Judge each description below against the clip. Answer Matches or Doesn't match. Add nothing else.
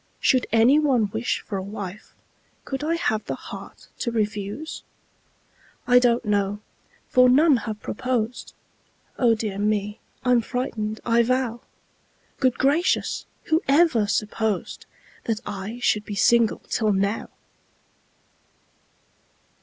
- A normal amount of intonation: Matches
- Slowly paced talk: Matches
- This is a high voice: Matches